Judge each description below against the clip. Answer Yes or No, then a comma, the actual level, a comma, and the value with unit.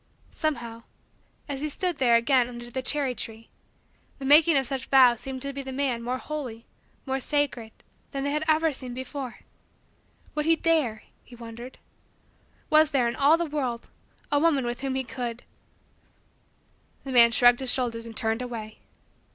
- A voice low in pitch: No, very high, 260 Hz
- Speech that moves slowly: No, average, 170 wpm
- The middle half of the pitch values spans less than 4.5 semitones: Yes, average, 3.2 semitones